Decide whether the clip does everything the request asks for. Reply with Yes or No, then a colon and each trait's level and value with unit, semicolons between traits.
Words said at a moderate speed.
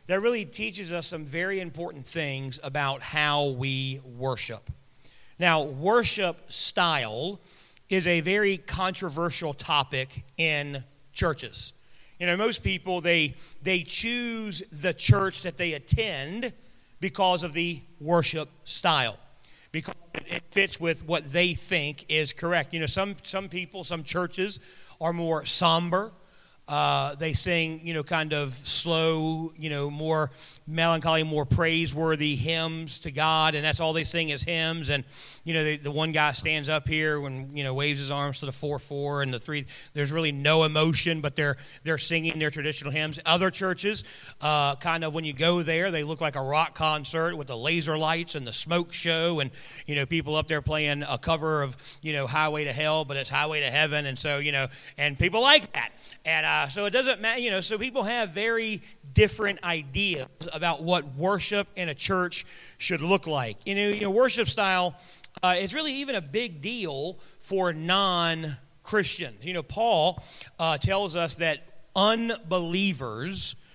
Yes: average, 170 wpm